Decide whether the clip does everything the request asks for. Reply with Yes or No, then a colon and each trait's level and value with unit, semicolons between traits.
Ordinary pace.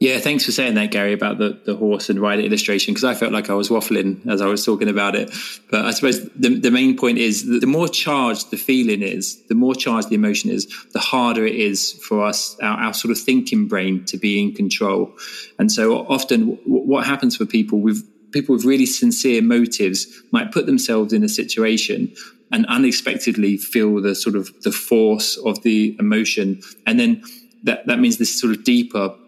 No: fast, 210 wpm